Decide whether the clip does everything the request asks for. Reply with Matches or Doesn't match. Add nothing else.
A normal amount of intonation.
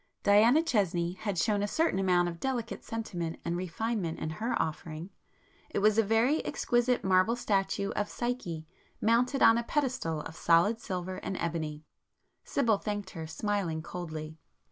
Matches